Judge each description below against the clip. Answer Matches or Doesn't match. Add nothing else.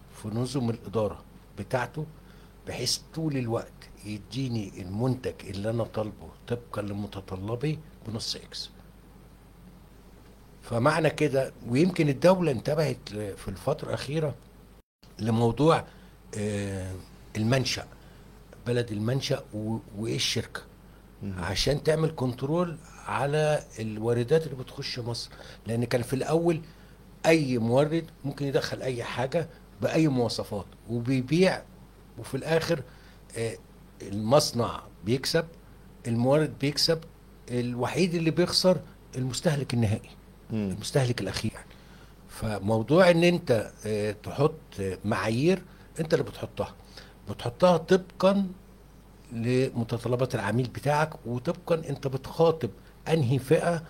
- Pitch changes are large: Matches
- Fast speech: Doesn't match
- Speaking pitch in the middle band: Doesn't match